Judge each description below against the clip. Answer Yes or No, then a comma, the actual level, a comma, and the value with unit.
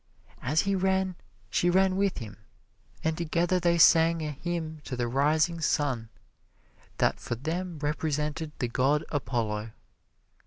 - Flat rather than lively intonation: No, average, 4.0 semitones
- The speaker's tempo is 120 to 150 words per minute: Yes, average, 140 wpm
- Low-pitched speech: No, medium, 155 Hz